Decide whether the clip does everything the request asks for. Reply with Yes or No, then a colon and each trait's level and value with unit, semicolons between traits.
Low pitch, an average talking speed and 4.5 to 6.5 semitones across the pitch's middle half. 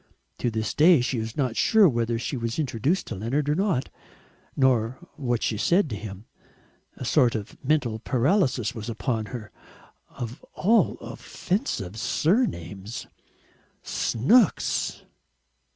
No: low, 120 Hz; slow, 130 wpm; wide, 5.5 semitones